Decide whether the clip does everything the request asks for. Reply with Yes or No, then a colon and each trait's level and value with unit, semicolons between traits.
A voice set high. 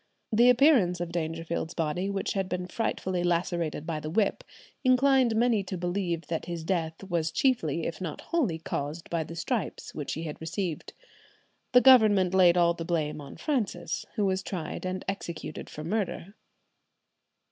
No: medium, 175 Hz